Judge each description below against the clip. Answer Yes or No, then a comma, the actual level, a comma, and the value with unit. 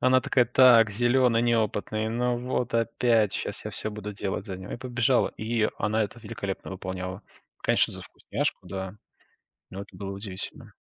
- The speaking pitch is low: Yes, low, 110 Hz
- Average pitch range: Yes, average, 3.3 semitones